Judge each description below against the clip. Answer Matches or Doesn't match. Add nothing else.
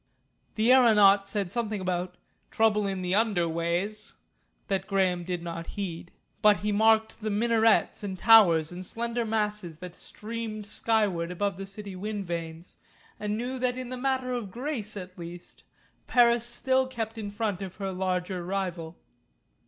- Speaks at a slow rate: Doesn't match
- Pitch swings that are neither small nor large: Matches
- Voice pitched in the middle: Doesn't match